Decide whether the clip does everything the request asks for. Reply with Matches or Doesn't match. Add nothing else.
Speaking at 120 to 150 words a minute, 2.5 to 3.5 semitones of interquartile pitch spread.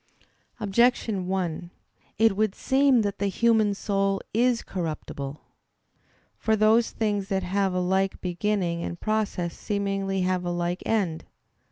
Matches